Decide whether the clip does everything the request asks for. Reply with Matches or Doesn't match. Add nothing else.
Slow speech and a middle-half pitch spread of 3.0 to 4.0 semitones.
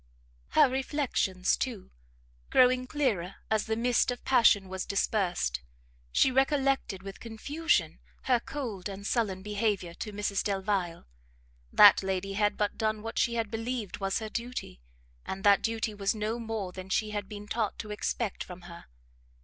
Doesn't match